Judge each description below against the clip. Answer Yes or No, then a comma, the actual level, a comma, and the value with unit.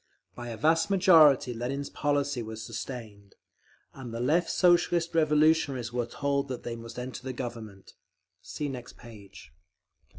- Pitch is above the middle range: No, low, 130 Hz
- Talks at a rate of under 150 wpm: Yes, average, 140 wpm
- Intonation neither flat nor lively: Yes, average, 4.5 semitones